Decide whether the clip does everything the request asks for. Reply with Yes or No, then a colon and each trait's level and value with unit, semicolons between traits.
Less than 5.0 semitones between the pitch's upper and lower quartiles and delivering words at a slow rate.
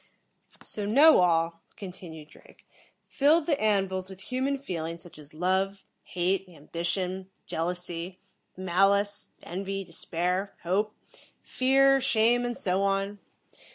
Yes: average, 3.2 semitones; slow, 115 wpm